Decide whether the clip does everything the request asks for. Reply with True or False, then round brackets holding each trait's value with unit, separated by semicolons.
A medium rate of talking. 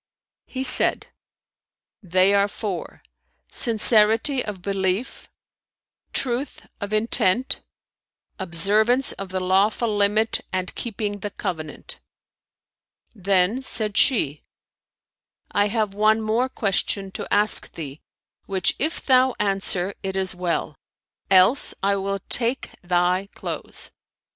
False (110 wpm)